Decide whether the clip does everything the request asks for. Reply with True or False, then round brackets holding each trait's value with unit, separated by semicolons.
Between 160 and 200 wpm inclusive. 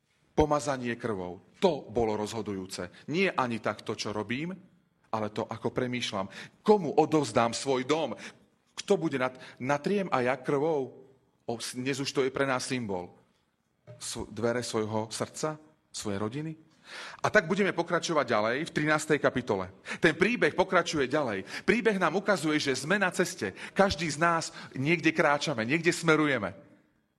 False (140 wpm)